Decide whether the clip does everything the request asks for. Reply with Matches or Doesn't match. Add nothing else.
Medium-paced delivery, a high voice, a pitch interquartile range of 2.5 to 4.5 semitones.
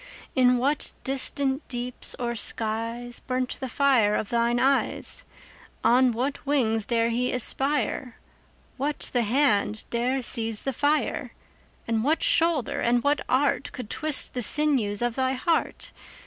Matches